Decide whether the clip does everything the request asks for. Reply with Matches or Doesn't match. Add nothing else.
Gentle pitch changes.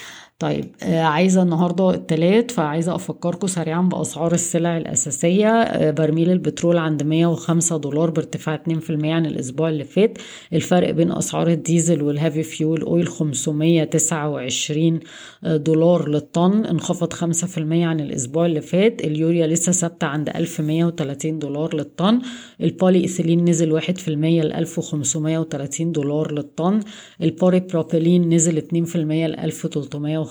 Matches